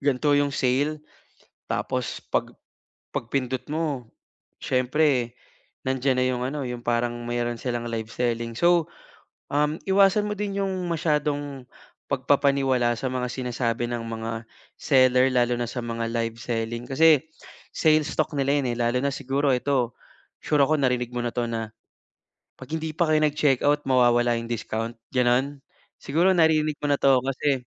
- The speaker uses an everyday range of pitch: Yes, average, 3.5 semitones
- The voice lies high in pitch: No, low, 130 Hz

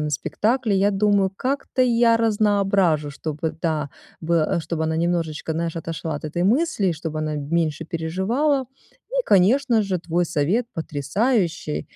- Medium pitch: Yes, medium, 175 Hz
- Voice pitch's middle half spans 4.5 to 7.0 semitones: Yes, average, 5.2 semitones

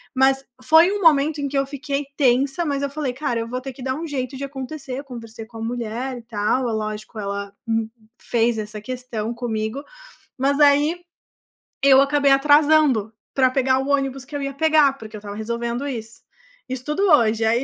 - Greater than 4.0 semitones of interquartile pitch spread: No, average, 3.7 semitones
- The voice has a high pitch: Yes, very high, 260 Hz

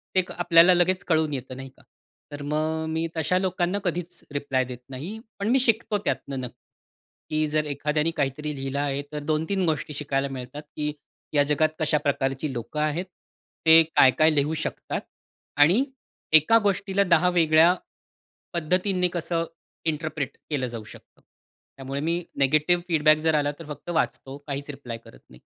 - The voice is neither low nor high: Yes, medium, 155 Hz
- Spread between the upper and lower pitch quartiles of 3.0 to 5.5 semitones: Yes, average, 3.6 semitones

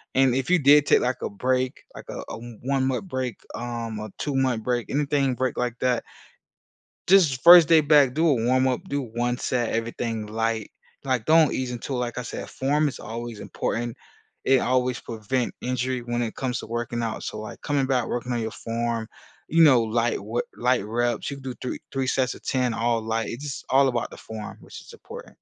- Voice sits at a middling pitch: No, low, 125 Hz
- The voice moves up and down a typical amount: No, narrow, 2.3 semitones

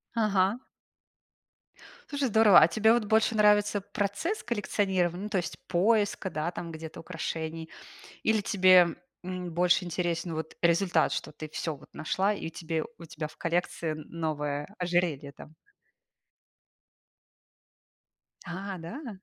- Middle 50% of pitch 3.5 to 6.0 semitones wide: Yes, average, 3.9 semitones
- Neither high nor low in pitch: Yes, medium, 180 Hz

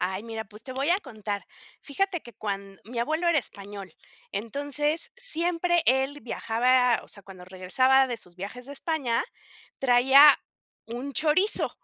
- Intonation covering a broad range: Yes, wide, 5.8 semitones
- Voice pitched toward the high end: Yes, very high, 255 Hz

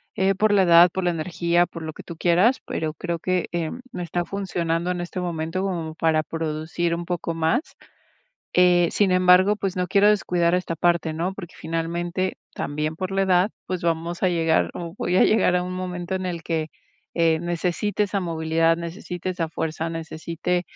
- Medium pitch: Yes, medium, 175 Hz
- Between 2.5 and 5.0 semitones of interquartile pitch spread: No, narrow, 1.9 semitones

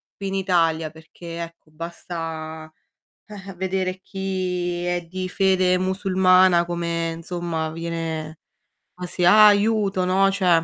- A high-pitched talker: No, medium, 180 Hz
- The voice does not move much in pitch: Yes, narrow, 2.2 semitones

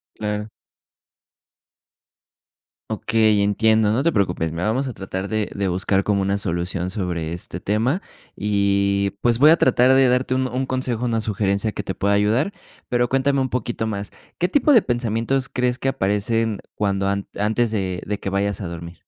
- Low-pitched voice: Yes, low, 105 Hz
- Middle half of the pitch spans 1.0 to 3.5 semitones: No, average, 3.9 semitones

